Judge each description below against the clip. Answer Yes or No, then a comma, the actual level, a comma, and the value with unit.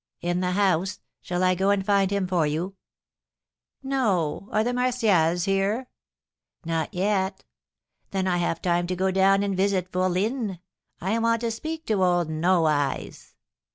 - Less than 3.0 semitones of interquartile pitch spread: Yes, narrow, 2.6 semitones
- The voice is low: No, high, 190 Hz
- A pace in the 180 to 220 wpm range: No, average, 155 wpm